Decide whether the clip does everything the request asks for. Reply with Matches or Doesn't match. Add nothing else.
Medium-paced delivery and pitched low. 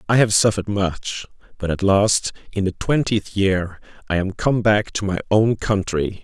Matches